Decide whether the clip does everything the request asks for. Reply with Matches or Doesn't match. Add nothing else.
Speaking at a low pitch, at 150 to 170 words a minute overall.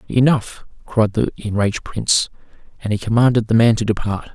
Matches